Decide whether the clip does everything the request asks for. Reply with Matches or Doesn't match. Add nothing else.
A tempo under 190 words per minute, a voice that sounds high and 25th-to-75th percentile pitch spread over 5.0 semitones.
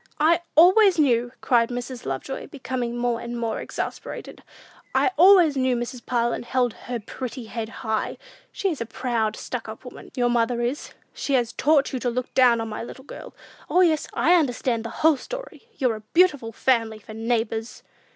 Doesn't match